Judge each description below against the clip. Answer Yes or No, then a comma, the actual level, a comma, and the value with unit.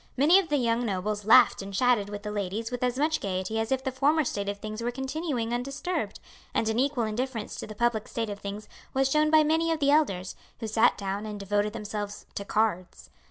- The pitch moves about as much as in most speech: Yes, average, 4.5 semitones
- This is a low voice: No, high, 225 Hz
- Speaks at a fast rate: Yes, fast, 225 wpm